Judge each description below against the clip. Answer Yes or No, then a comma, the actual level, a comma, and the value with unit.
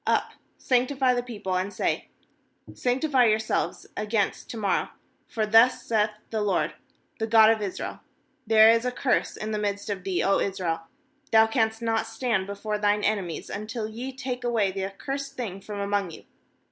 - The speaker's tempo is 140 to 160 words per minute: No, average, 175 wpm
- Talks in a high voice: Yes, high, 220 Hz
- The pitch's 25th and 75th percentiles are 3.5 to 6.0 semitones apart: No, average, 3.0 semitones